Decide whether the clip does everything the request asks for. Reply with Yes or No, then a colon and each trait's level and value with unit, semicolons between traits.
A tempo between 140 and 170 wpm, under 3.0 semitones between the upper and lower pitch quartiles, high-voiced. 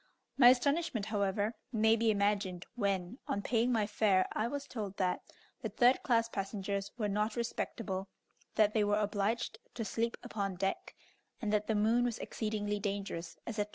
Yes: average, 165 wpm; narrow, 2.4 semitones; high, 210 Hz